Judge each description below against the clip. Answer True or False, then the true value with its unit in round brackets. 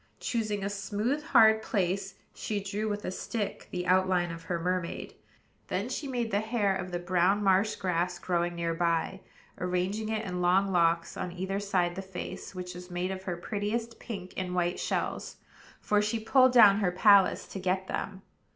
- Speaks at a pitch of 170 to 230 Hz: True (190 Hz)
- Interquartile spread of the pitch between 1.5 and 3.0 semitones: True (2.6 semitones)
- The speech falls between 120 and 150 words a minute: False (185 wpm)